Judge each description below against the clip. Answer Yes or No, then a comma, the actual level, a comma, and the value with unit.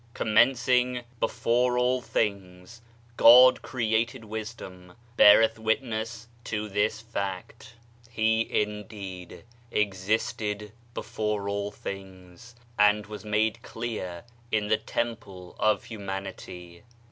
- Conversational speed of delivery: No, slow, 110 wpm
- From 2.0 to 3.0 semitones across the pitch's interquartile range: Yes, narrow, 2.5 semitones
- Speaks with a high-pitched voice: No, low, 110 Hz